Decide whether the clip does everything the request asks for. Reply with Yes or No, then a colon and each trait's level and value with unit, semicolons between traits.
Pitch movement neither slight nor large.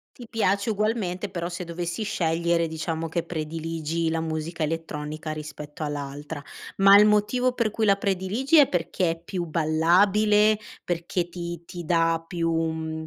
Yes: average, 3.6 semitones